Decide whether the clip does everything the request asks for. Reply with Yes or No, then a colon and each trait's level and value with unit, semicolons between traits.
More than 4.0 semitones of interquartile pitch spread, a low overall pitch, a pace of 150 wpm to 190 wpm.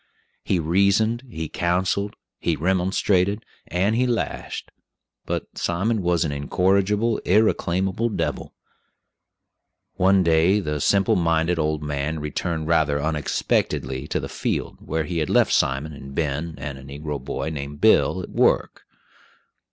No: average, 4.4 semitones; very low, 85 Hz; slow, 135 wpm